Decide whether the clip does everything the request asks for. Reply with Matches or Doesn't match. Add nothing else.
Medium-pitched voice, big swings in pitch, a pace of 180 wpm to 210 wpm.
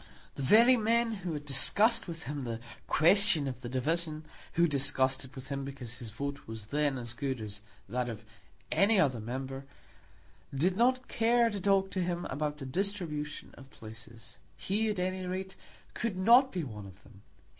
Matches